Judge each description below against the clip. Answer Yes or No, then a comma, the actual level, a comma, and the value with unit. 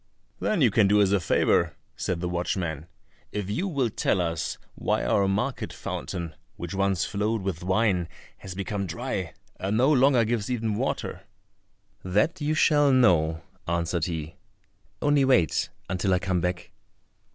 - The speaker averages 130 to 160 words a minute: Yes, average, 155 wpm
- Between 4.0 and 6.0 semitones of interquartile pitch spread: Yes, average, 5.1 semitones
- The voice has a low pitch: Yes, low, 100 Hz